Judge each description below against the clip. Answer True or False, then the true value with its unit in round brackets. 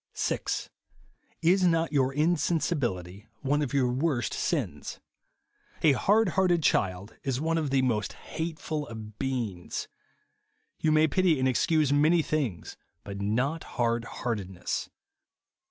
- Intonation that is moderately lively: False (5.7 semitones)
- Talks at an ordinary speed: False (125 wpm)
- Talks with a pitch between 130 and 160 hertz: True (140 Hz)